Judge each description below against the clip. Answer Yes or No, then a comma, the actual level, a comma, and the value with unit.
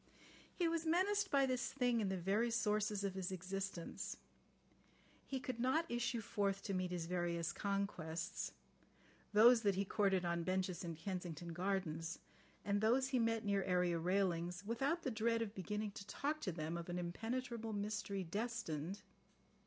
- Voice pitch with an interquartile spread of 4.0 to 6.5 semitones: Yes, average, 4.5 semitones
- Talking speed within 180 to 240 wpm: No, average, 160 wpm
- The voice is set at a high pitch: Yes, high, 200 Hz